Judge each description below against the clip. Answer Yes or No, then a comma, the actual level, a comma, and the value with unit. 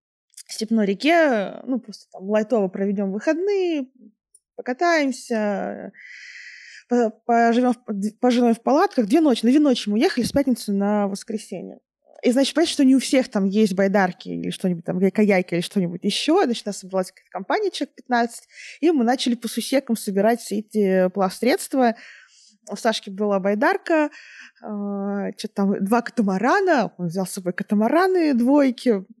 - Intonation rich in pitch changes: No, average, 4.5 semitones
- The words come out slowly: No, average, 155 wpm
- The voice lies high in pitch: Yes, high, 225 Hz